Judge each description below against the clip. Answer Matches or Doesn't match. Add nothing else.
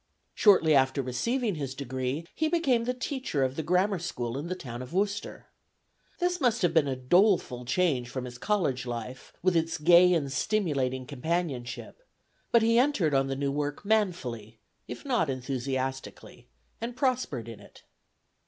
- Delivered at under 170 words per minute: Matches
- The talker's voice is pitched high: Doesn't match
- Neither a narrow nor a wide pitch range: Doesn't match